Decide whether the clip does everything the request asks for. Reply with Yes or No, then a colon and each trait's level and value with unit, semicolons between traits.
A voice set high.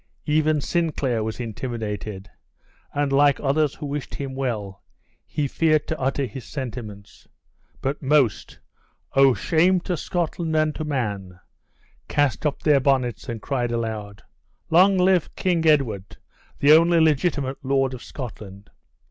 No: low, 135 Hz